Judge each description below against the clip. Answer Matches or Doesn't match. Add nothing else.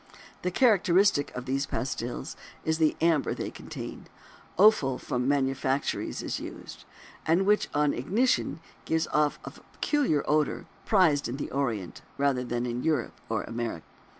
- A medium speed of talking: Matches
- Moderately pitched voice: Matches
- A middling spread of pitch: Matches